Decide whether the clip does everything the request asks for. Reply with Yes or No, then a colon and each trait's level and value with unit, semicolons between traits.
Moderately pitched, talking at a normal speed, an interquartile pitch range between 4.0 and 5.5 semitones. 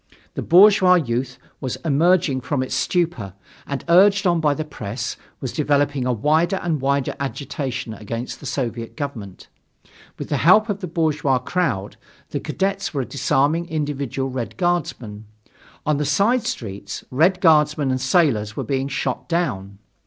Yes: medium, 145 Hz; average, 150 wpm; average, 5.1 semitones